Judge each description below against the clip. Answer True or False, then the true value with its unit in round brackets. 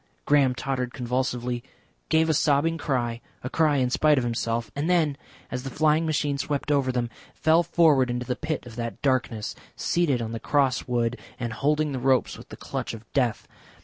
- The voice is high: False (130 Hz)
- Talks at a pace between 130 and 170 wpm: False (190 wpm)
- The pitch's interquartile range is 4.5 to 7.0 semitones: False (3.6 semitones)